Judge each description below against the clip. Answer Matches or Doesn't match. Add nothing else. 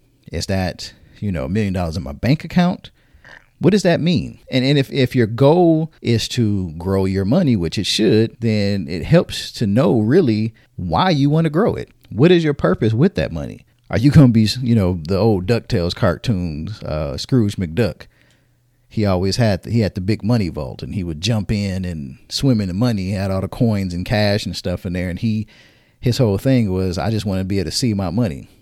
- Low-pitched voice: Matches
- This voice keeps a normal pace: Doesn't match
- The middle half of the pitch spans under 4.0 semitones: Doesn't match